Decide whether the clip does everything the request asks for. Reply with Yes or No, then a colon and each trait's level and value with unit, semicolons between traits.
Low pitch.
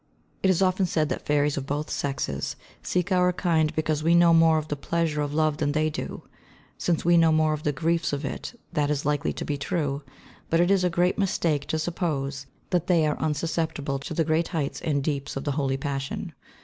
No: medium, 155 Hz